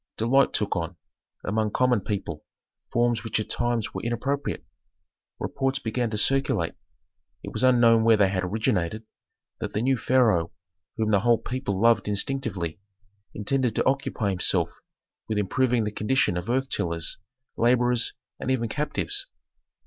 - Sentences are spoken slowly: No, average, 145 wpm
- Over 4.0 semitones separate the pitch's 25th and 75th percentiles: No, average, 3.6 semitones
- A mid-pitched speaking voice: No, low, 115 Hz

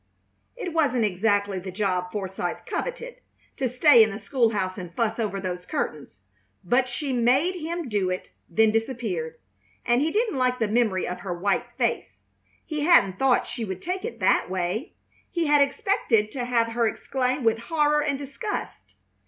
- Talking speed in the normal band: Yes, average, 175 wpm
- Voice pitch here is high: Yes, high, 235 Hz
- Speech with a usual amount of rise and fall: No, wide, 6.3 semitones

